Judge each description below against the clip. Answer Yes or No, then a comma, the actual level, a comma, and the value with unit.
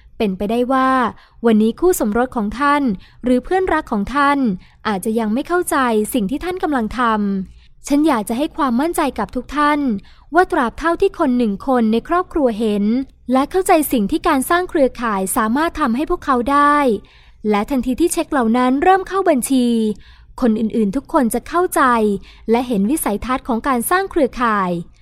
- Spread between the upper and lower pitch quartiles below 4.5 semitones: No, average, 5.2 semitones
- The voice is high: Yes, very high, 260 Hz